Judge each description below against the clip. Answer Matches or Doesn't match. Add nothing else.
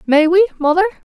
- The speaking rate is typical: Matches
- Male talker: Doesn't match